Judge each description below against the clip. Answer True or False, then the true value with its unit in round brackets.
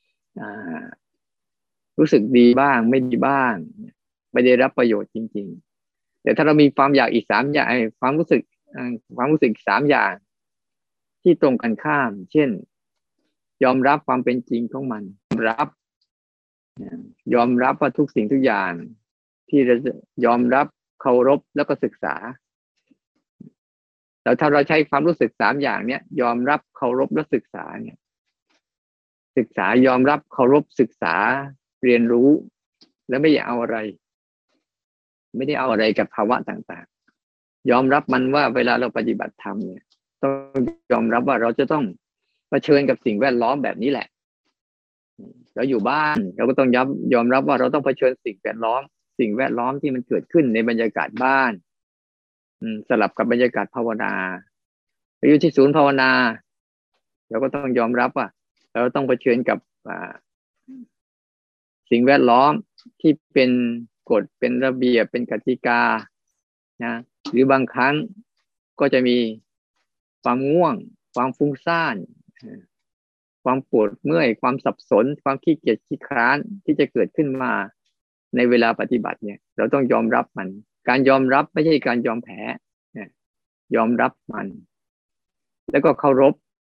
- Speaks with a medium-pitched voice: False (130 Hz)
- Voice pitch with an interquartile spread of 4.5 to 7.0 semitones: False (3.3 semitones)